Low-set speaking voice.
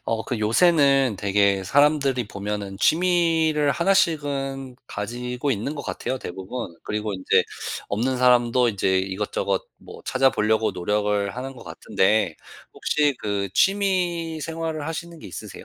Yes: low, 125 Hz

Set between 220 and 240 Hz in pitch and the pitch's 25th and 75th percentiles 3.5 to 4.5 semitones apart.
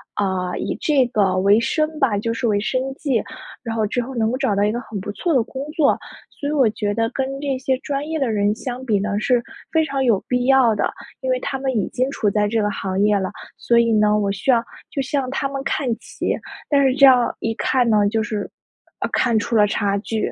Yes: high, 235 Hz; average, 4.2 semitones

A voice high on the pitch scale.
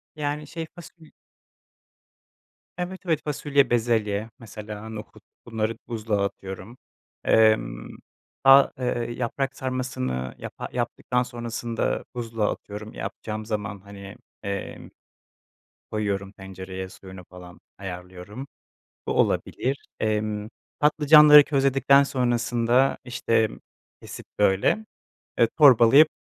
No: low, 115 Hz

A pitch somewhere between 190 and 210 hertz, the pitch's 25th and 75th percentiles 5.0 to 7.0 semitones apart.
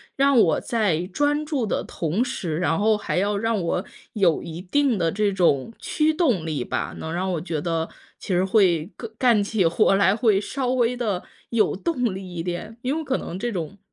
Yes: high, 200 Hz; wide, 5.5 semitones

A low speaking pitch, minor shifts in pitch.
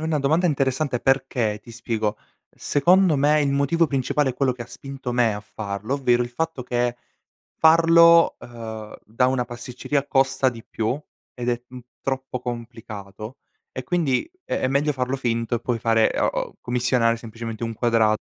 No: low, 125 Hz; average, 3.1 semitones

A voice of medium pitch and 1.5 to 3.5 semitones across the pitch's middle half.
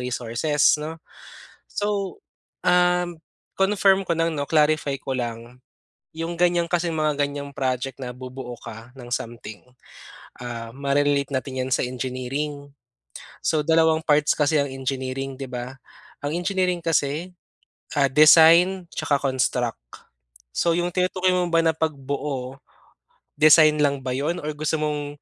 No: medium, 145 Hz; average, 4.1 semitones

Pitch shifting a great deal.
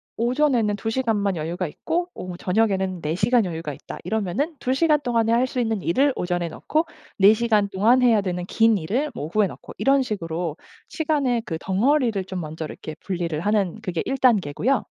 Yes: wide, 6.0 semitones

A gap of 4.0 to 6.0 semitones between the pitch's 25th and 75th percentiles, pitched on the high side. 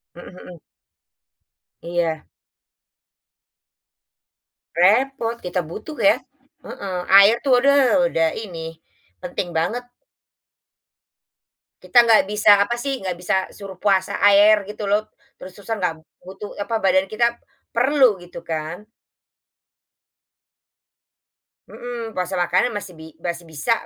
Yes: average, 4.7 semitones; high, 200 Hz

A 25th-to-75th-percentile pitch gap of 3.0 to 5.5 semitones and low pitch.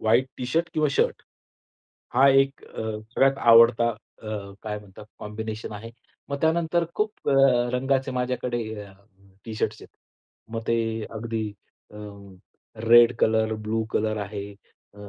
Yes: average, 3.7 semitones; low, 115 Hz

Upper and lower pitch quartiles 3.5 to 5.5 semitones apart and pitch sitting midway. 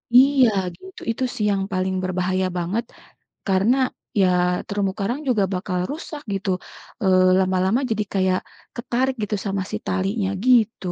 No: average, 4.1 semitones; high, 195 Hz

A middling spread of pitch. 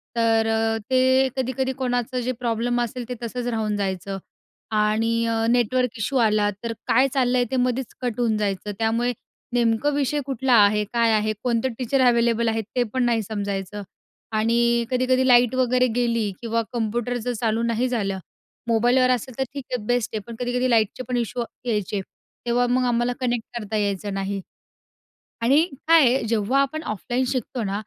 No: narrow, 2.3 semitones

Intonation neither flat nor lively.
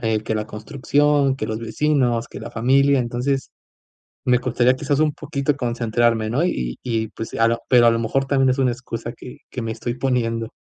Yes: average, 3.0 semitones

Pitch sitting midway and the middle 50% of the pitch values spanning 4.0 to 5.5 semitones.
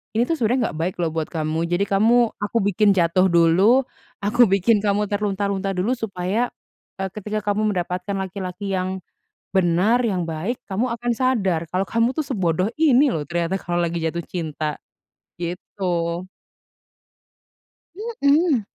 No: high, 195 Hz; average, 4.5 semitones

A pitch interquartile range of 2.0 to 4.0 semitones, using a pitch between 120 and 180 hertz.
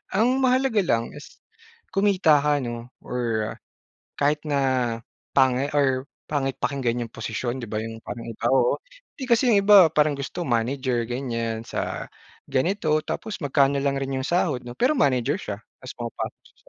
No: average, 4.5 semitones; low, 135 Hz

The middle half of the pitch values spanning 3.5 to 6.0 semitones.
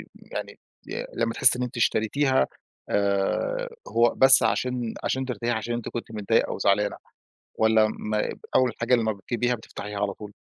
No: average, 2.8 semitones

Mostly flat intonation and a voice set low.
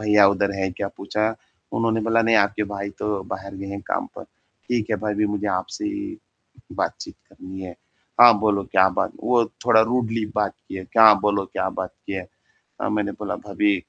Yes: narrow, 2.3 semitones; low, 105 Hz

